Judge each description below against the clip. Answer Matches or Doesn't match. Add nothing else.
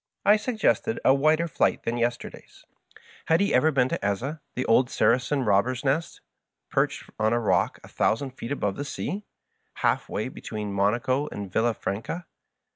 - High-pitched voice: Doesn't match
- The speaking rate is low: Doesn't match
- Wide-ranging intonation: Matches